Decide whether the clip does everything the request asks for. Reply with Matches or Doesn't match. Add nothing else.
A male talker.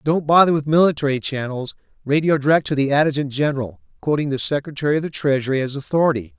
Matches